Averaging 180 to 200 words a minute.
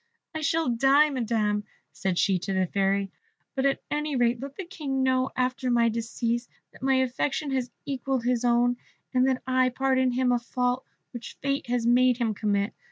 Yes: average, 185 wpm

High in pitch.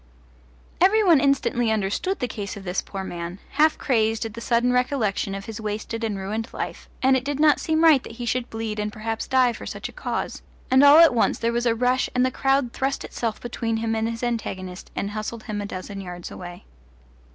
Yes: high, 230 Hz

